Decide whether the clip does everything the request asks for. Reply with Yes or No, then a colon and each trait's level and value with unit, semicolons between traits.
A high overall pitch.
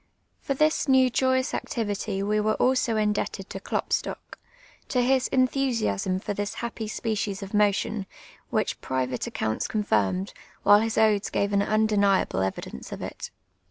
Yes: high, 210 Hz